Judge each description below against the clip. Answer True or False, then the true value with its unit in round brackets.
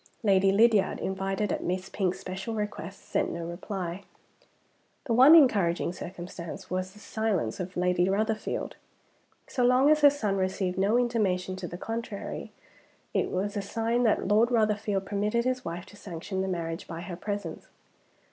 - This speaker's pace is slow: False (160 wpm)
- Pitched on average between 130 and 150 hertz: False (195 Hz)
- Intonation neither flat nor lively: True (3.3 semitones)